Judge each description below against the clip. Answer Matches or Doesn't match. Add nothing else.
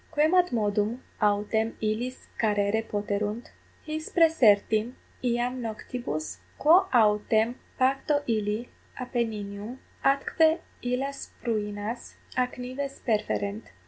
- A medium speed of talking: Doesn't match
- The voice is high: Matches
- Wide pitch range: Doesn't match